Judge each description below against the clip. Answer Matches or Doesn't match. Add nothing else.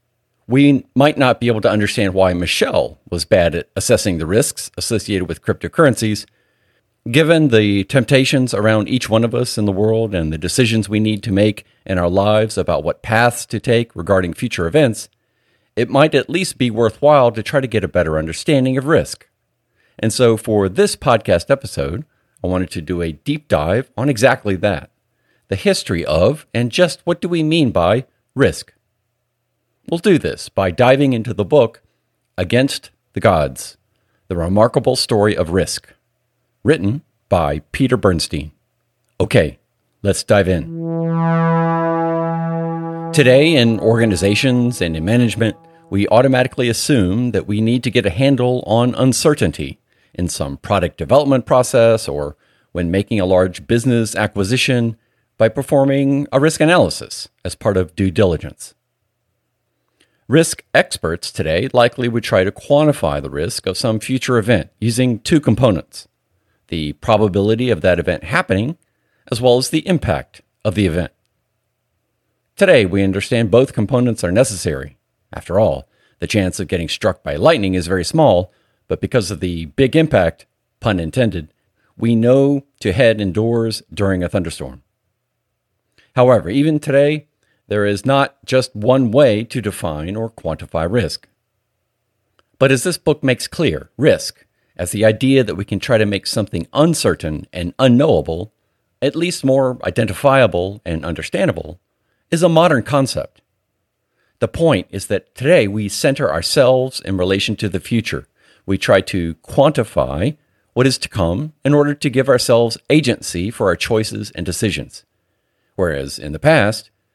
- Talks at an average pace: Matches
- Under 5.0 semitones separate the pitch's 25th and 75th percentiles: Doesn't match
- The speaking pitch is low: Matches